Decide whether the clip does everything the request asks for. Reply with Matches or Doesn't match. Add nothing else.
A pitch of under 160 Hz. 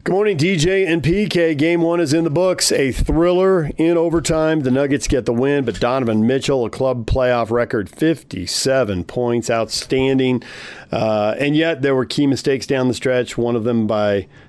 Matches